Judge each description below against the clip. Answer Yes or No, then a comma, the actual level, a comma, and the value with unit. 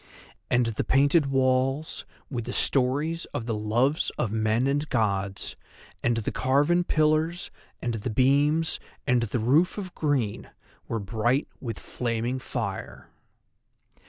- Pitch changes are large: No, average, 4.2 semitones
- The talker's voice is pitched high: No, low, 130 Hz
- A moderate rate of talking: No, slow, 130 wpm